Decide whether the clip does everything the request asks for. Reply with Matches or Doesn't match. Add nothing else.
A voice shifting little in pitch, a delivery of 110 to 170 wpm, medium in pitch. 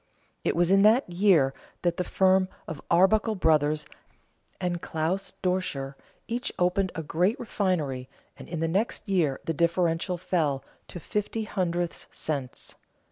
Doesn't match